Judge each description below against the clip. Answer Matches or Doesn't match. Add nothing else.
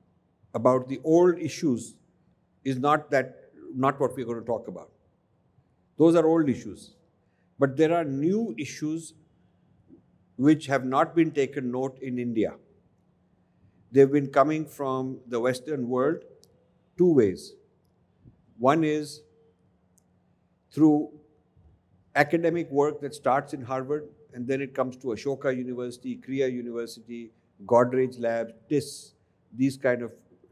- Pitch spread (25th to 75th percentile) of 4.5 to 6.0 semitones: Doesn't match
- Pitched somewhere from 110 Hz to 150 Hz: Matches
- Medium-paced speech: Doesn't match